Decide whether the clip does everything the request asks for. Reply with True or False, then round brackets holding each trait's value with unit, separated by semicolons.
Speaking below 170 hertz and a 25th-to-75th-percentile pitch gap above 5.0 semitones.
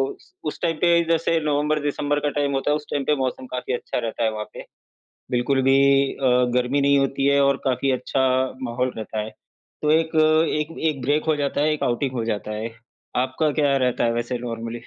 False (135 Hz; 3.2 semitones)